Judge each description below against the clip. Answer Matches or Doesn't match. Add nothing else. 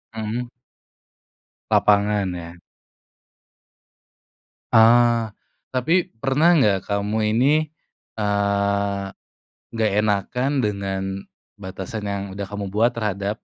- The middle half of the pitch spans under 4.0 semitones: Matches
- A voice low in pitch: Matches